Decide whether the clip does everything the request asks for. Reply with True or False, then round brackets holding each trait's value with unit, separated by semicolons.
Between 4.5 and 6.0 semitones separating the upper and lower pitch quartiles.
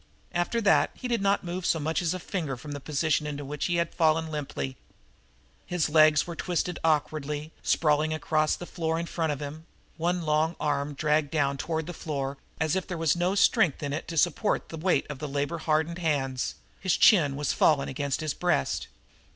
False (2.7 semitones)